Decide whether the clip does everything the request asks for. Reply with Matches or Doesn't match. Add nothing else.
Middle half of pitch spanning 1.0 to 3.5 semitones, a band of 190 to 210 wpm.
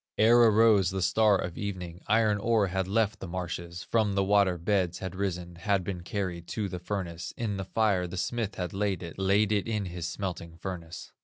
Matches